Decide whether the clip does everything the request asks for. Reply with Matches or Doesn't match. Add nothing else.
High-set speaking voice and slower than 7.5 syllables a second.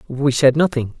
Doesn't match